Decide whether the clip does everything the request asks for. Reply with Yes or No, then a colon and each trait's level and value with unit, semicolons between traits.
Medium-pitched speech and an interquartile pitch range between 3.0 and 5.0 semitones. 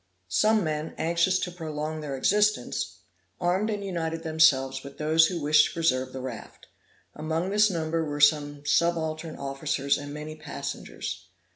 No: medium, 155 Hz; narrow, 2.6 semitones